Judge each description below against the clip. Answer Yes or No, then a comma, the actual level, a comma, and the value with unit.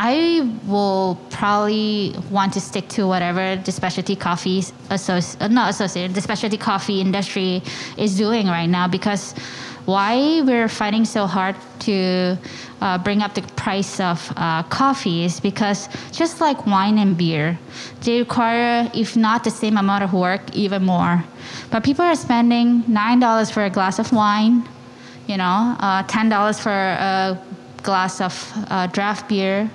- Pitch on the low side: No, high, 200 Hz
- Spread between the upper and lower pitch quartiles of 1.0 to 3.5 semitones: Yes, average, 2.9 semitones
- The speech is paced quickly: No, average, 155 wpm